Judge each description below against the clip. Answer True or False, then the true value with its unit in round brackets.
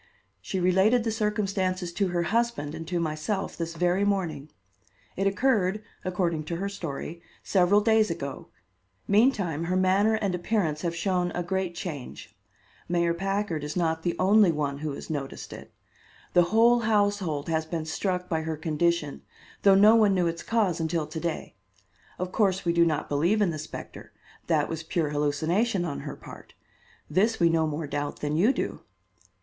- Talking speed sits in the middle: True (175 wpm)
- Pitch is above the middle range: False (175 Hz)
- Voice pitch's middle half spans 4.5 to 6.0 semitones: False (3.8 semitones)